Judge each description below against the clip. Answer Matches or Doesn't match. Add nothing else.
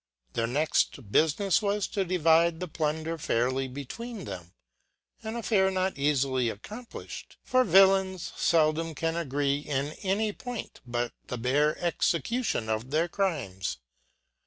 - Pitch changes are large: Matches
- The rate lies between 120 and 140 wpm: Matches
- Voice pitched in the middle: Matches